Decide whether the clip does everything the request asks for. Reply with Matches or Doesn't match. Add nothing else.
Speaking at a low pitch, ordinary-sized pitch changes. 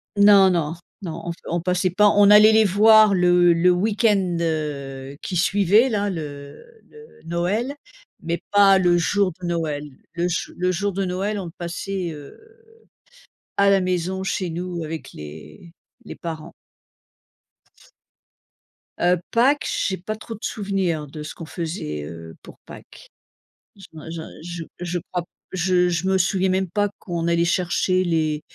Doesn't match